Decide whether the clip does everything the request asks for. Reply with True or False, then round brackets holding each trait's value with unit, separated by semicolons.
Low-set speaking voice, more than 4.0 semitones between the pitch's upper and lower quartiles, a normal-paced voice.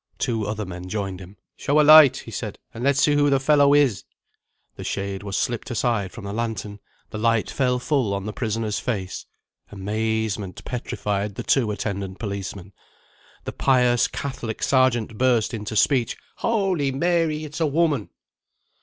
True (115 Hz; 5.1 semitones; 165 wpm)